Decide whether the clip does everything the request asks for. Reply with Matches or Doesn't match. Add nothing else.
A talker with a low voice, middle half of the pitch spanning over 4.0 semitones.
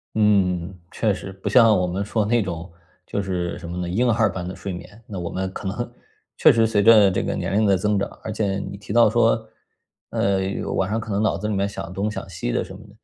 Doesn't match